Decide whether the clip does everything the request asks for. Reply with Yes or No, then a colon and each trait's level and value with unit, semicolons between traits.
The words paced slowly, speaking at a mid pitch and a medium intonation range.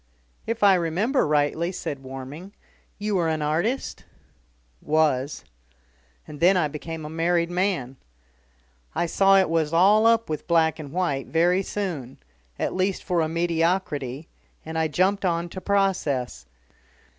No: average, 145 wpm; medium, 170 Hz; average, 3.7 semitones